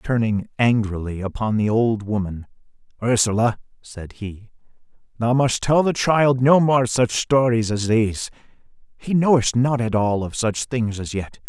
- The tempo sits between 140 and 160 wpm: Yes, average, 155 wpm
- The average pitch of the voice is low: Yes, low, 115 Hz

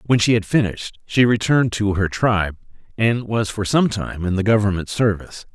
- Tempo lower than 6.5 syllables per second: Yes, 5.5 syllables/s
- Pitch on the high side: No, low, 105 Hz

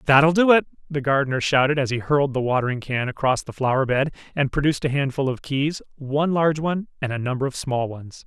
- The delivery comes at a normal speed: No, fast, 220 wpm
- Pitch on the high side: No, medium, 140 Hz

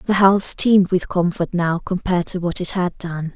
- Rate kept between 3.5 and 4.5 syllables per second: No, 5.2 syllables/s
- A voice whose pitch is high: No, medium, 180 Hz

